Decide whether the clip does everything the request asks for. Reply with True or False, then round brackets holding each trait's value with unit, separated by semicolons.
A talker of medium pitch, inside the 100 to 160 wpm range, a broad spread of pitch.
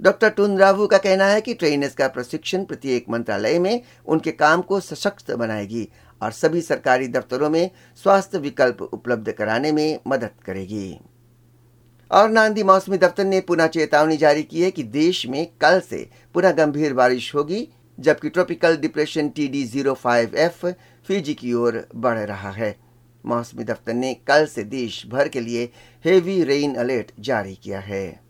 True (150 Hz; 155 wpm; 7.1 semitones)